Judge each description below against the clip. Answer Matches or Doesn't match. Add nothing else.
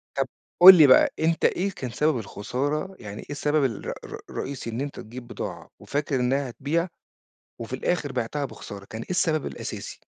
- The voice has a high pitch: Doesn't match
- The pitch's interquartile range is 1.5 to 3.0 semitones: Doesn't match